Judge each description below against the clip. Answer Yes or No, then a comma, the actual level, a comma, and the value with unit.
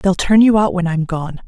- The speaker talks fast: Yes, fast, 285 wpm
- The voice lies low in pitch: No, medium, 185 Hz